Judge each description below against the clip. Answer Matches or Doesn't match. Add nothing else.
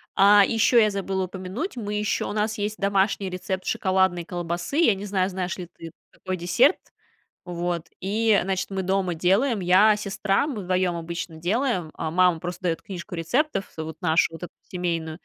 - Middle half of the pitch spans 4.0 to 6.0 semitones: Doesn't match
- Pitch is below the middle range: Doesn't match